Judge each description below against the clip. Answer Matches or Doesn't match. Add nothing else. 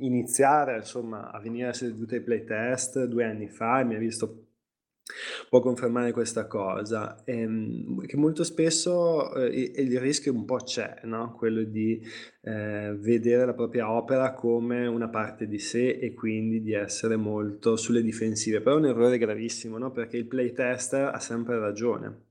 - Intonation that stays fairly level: Matches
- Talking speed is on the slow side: Doesn't match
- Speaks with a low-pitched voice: Matches